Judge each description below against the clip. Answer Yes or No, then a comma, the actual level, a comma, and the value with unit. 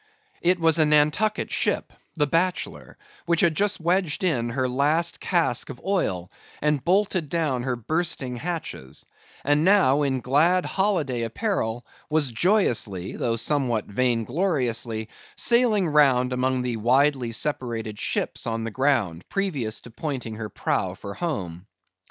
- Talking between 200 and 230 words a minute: No, average, 140 wpm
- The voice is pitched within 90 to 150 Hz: Yes, medium, 140 Hz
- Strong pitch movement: Yes, wide, 6.3 semitones